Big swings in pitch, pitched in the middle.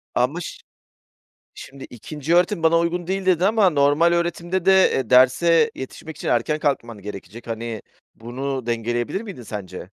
Yes: wide, 6.3 semitones; medium, 145 Hz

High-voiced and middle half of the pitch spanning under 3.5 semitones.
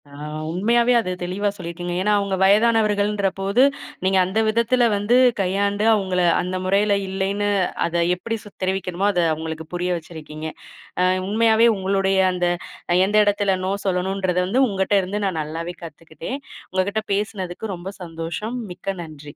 Yes: high, 195 Hz; average, 2.7 semitones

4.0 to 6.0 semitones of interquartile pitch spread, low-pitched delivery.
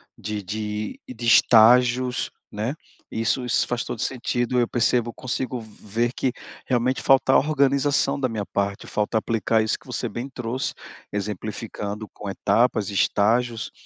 No: average, 2.9 semitones; low, 115 Hz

